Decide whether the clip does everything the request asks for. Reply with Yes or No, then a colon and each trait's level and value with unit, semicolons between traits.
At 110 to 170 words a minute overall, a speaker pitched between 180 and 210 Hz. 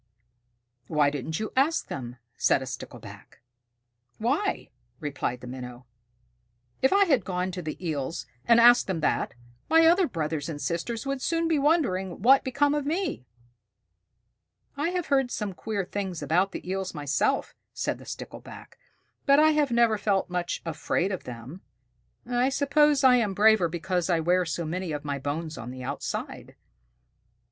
Yes: average, 165 wpm; high, 190 Hz